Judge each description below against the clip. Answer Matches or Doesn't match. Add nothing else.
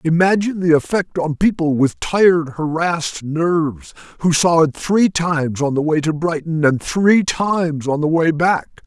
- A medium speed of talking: Matches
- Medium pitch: Matches